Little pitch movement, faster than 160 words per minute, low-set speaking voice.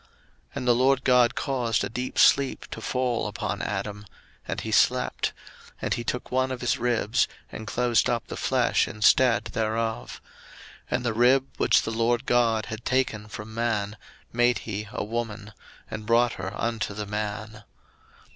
Yes: narrow, 2.3 semitones; average, 170 wpm; low, 115 Hz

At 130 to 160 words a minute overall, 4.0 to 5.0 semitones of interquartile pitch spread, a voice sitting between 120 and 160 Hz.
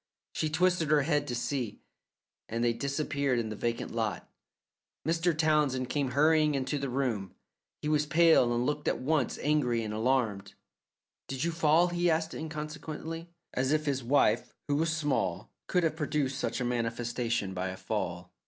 No: average, 170 wpm; average, 4.3 semitones; medium, 140 Hz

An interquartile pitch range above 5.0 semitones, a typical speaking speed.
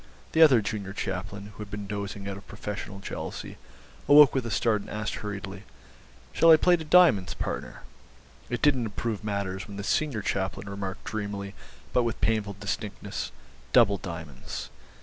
No: average, 2.8 semitones; average, 165 wpm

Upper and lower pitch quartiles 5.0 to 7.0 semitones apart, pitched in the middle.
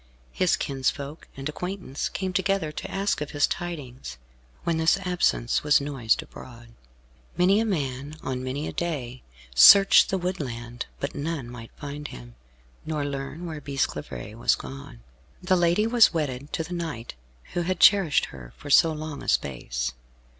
Yes: wide, 5.4 semitones; medium, 145 Hz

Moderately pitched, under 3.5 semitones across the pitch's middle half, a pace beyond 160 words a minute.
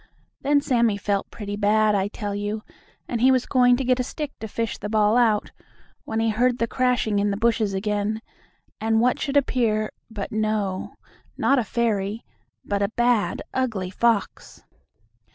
No: high, 220 Hz; average, 3.0 semitones; average, 170 wpm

